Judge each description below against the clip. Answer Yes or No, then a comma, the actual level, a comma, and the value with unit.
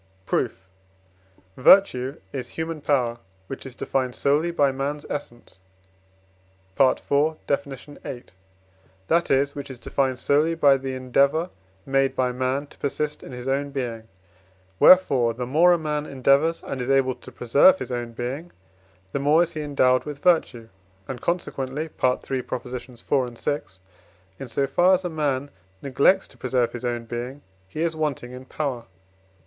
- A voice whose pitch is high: No, low, 135 Hz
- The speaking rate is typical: Yes, average, 155 wpm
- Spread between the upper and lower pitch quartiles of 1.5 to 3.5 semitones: Yes, average, 2.9 semitones